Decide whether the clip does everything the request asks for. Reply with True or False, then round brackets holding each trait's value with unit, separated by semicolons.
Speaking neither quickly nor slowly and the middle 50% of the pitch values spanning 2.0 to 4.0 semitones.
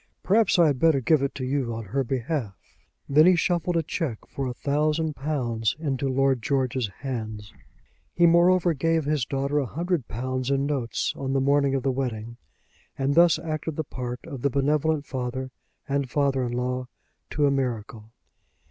True (180 wpm; 3.4 semitones)